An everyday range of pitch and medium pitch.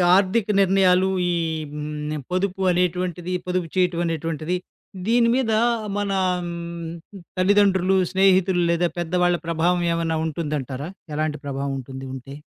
Yes: average, 3.0 semitones; medium, 175 Hz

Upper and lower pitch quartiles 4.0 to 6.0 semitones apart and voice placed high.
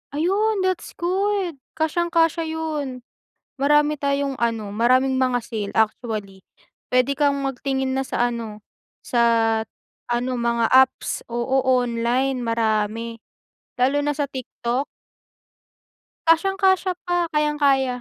Yes: average, 4.6 semitones; very high, 265 Hz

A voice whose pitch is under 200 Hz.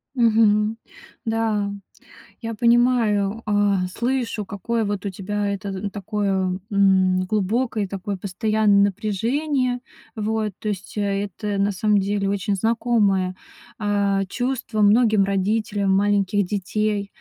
No: high, 205 Hz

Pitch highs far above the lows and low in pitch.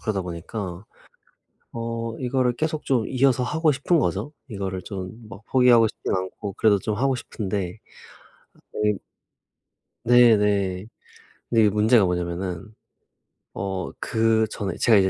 No: average, 4.2 semitones; low, 110 Hz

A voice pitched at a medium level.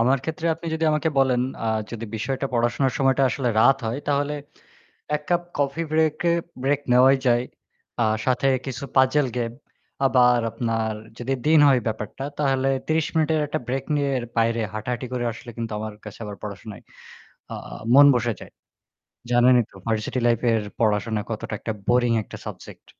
No: low, 125 Hz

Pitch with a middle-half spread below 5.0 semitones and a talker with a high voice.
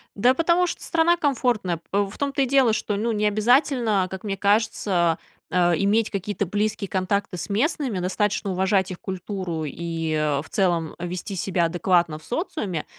Yes: average, 4.1 semitones; high, 200 Hz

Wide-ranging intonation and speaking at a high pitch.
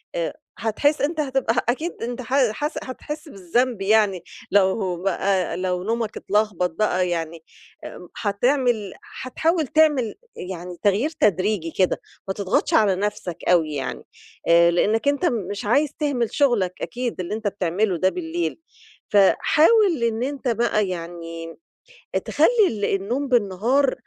Yes: wide, 5.9 semitones; high, 210 Hz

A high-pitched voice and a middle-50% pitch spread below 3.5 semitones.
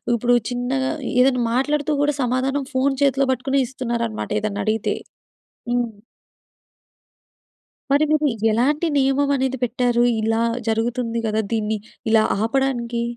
Yes: very high, 250 Hz; average, 2.7 semitones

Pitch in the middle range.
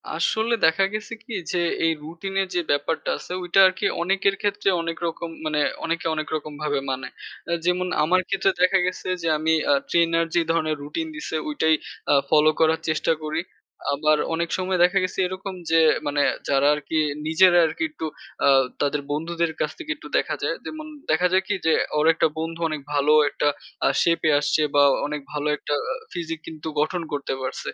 Yes: medium, 165 Hz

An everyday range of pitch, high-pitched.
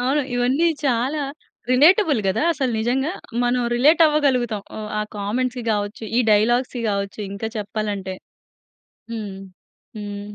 Yes: average, 4.3 semitones; high, 240 Hz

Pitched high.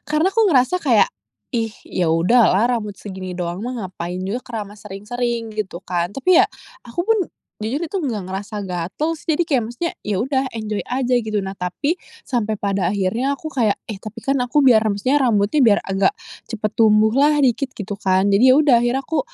Yes: high, 220 Hz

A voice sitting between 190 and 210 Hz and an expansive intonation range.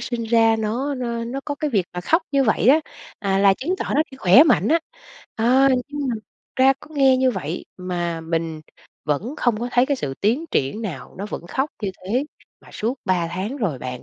No: high, 225 Hz; wide, 6.5 semitones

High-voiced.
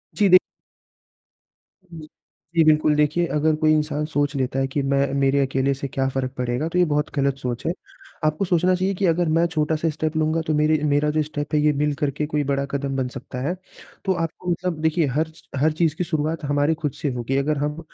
No: medium, 150 Hz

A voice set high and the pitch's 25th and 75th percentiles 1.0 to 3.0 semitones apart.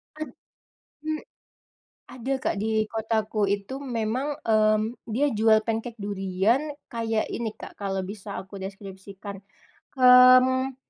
No: high, 220 Hz; average, 3.7 semitones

